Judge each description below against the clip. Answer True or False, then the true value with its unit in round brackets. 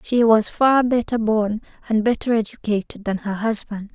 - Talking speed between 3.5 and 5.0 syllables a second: True (4.8 syllables/s)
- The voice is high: True (220 Hz)